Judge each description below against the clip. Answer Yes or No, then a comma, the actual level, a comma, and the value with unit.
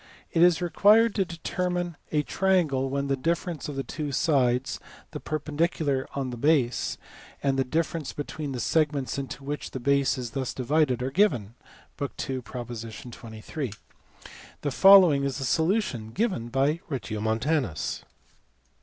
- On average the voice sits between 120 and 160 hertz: Yes, medium, 140 Hz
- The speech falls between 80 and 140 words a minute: No, average, 150 wpm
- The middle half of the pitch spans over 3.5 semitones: Yes, average, 4.2 semitones